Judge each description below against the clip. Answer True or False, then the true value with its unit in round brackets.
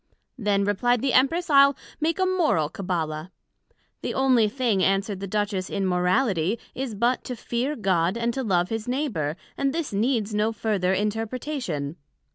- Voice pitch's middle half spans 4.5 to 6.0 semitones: True (5.4 semitones)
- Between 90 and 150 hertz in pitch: False (215 Hz)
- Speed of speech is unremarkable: True (160 wpm)